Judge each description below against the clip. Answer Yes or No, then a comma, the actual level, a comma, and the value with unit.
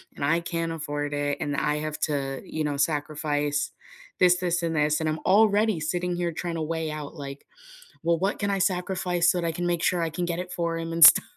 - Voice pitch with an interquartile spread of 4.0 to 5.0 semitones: No, average, 2.9 semitones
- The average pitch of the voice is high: No, medium, 165 Hz